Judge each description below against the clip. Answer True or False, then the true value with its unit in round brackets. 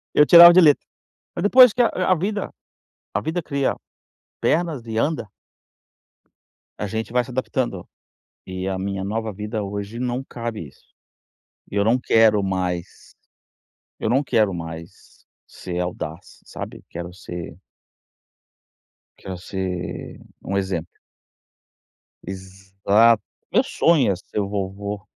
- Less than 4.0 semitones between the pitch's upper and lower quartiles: False (5.2 semitones)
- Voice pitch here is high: False (105 Hz)